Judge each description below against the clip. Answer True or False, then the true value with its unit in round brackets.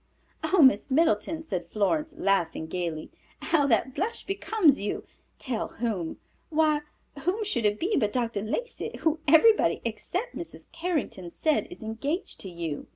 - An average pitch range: False (8.2 semitones)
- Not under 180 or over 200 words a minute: False (150 wpm)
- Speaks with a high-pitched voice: True (270 Hz)